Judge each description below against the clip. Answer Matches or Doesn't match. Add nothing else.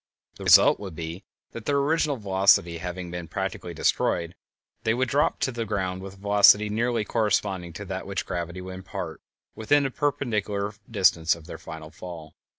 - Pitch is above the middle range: Doesn't match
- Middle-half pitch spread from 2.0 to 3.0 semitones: Doesn't match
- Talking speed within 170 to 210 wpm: Matches